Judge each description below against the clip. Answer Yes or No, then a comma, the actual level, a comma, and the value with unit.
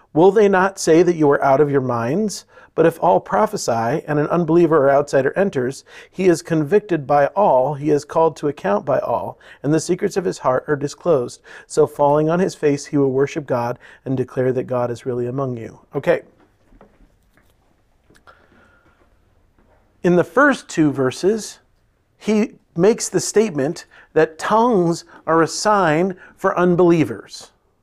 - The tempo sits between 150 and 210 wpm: Yes, average, 160 wpm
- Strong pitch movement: Yes, wide, 5.7 semitones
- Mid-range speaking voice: Yes, medium, 155 Hz